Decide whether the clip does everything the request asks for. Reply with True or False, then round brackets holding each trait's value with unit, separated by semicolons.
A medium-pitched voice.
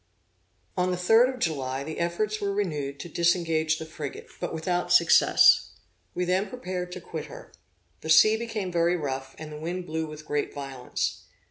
True (170 Hz)